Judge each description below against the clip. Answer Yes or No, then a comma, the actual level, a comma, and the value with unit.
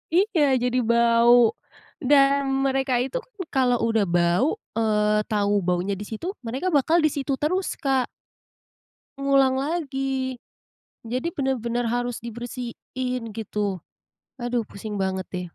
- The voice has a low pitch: No, high, 245 Hz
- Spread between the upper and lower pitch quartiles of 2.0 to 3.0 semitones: No, average, 3.6 semitones